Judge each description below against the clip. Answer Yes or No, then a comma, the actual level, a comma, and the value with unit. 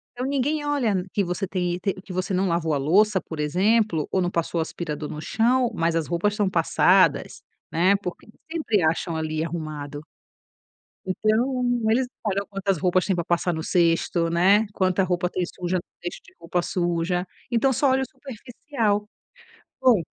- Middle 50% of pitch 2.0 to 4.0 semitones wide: No, average, 4.4 semitones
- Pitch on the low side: No, medium, 185 Hz